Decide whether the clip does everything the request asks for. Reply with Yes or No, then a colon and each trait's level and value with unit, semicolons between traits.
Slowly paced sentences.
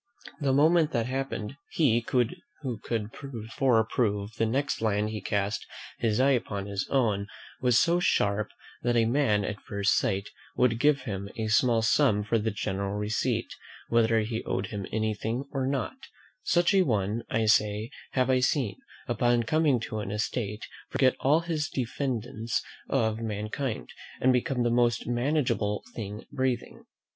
No: average, 160 wpm